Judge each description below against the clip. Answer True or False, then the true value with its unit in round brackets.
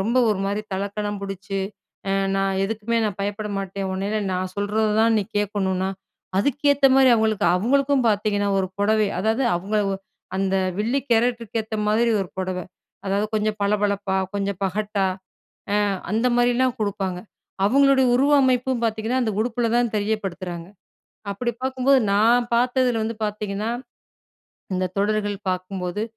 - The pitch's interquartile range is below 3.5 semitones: True (3.1 semitones)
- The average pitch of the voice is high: True (210 Hz)